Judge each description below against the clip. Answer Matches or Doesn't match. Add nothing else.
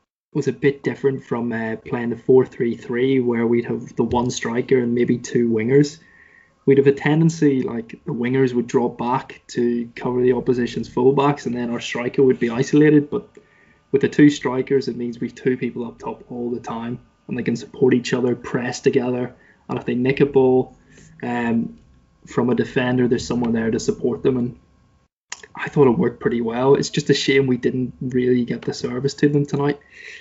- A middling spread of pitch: Doesn't match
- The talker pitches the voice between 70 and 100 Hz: Doesn't match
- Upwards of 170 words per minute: Matches